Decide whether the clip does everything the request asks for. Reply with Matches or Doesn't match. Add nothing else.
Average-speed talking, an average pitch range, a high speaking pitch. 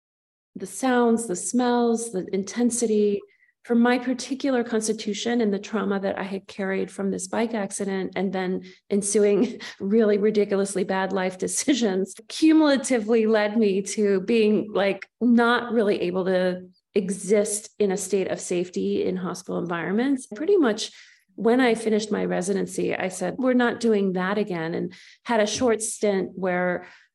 Matches